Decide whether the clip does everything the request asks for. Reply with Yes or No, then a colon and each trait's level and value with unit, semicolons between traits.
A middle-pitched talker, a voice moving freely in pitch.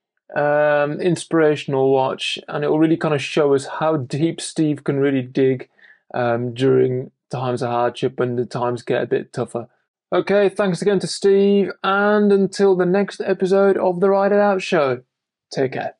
Yes: medium, 155 Hz; wide, 6.5 semitones